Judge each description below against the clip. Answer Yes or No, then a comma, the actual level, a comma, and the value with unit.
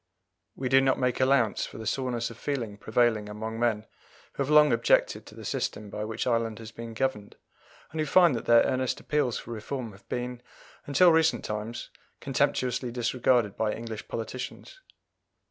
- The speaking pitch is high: No, low, 120 Hz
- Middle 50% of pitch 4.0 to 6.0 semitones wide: No, average, 3.0 semitones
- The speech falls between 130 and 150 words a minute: No, average, 175 wpm